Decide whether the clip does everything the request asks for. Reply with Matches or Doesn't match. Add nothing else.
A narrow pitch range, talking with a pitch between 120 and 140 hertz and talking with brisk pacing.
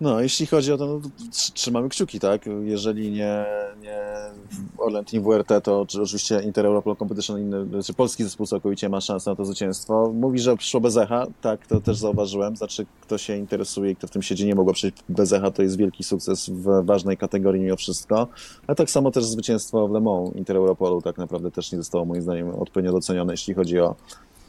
Doesn't match